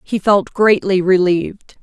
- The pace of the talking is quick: No, slow, 130 wpm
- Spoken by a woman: Yes, female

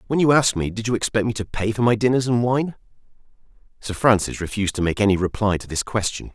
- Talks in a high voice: No, low, 110 Hz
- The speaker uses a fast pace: Yes, fast, 235 wpm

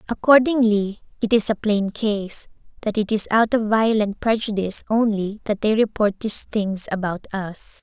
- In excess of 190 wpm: No, average, 160 wpm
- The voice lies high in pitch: Yes, high, 210 Hz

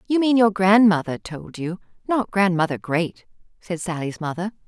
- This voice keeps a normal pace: Yes, average, 155 wpm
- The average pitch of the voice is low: No, high, 190 Hz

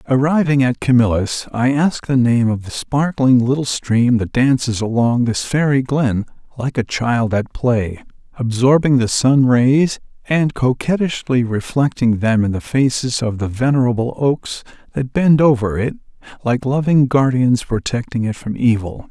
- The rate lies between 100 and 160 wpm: Yes, average, 155 wpm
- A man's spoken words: Yes, male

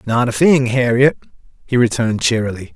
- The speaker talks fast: No, average, 150 wpm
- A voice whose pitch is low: Yes, low, 120 Hz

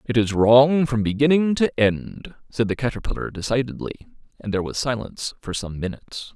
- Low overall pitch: Yes, low, 120 Hz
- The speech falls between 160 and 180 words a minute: Yes, average, 170 wpm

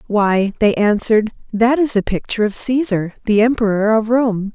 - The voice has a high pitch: Yes, high, 220 Hz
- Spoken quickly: No, average, 170 wpm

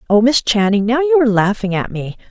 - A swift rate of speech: Yes, fast, 235 wpm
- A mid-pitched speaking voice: No, high, 220 Hz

